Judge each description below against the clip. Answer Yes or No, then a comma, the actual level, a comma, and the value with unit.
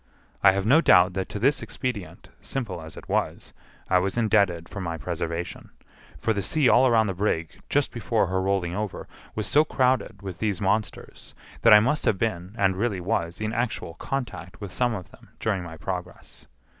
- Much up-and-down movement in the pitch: No, average, 4.0 semitones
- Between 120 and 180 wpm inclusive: No, average, 195 wpm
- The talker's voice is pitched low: Yes, low, 100 Hz